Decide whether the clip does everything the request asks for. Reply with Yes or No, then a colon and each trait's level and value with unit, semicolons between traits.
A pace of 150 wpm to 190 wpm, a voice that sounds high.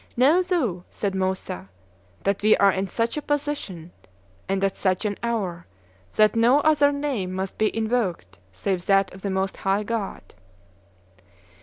Yes: average, 155 wpm; high, 200 Hz